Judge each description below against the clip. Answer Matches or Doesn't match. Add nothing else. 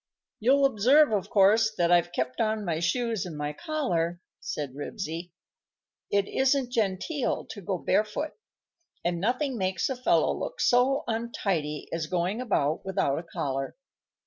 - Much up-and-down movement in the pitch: Matches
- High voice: Matches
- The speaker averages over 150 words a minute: Doesn't match